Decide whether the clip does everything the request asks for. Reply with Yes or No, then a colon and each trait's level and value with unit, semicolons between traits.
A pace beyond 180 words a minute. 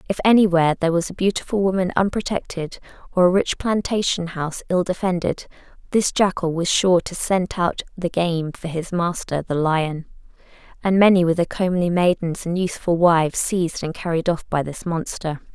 No: average, 175 wpm